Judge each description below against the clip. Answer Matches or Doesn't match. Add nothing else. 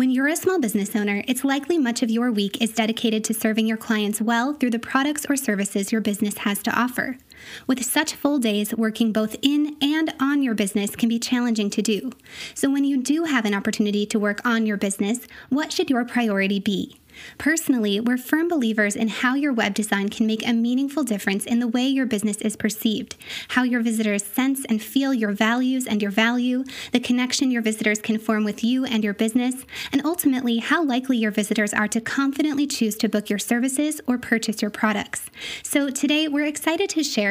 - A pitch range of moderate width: Matches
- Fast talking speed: Matches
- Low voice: Doesn't match